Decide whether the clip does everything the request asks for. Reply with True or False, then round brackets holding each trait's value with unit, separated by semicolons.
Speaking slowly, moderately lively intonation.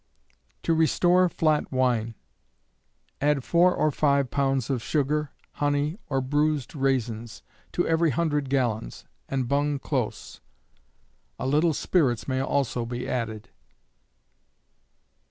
True (115 wpm; 3.3 semitones)